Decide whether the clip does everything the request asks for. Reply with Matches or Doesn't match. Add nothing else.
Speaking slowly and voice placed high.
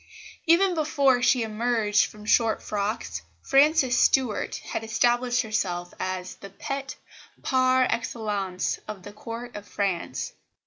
Matches